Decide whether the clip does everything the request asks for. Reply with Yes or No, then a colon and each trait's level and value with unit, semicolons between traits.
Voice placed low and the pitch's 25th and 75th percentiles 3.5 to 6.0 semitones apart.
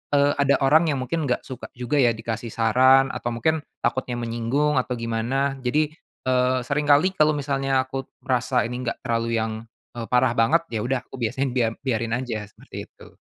No: low, 130 Hz; average, 3.0 semitones